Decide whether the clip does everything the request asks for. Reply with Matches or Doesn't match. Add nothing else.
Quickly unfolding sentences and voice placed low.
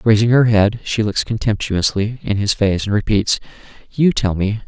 Doesn't match